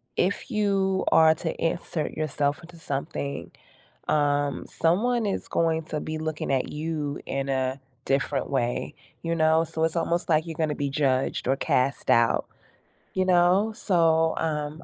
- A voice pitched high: No, medium, 160 Hz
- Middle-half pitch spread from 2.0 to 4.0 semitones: Yes, average, 2.9 semitones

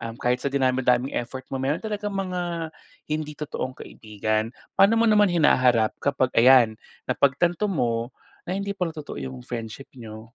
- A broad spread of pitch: Yes, wide, 6.7 semitones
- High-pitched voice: No, low, 135 Hz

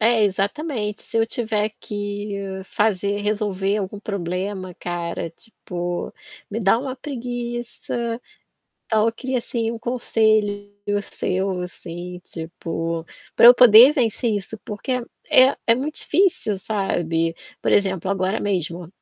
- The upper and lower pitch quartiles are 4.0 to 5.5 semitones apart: No, average, 3.6 semitones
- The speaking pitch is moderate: No, high, 205 Hz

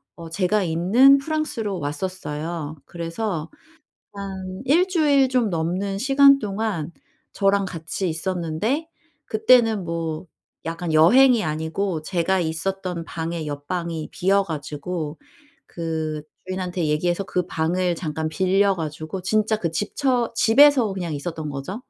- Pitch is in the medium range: Yes, medium, 180 Hz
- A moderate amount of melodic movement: Yes, average, 4.7 semitones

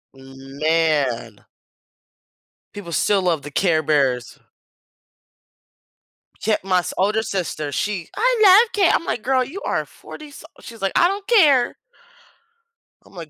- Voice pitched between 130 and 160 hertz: No, high, 190 Hz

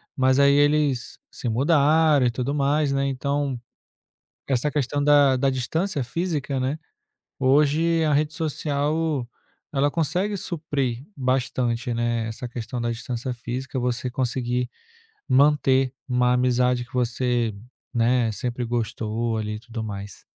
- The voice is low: Yes, low, 130 Hz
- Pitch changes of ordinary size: Yes, average, 3.2 semitones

